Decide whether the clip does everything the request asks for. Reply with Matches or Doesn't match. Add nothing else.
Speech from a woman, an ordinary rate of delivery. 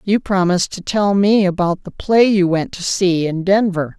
Doesn't match